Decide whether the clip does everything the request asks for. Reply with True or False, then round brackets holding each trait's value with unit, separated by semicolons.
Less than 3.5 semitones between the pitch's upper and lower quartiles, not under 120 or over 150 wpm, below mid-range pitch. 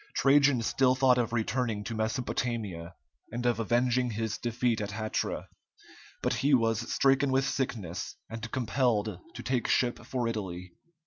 True (2.7 semitones; 145 wpm; 120 Hz)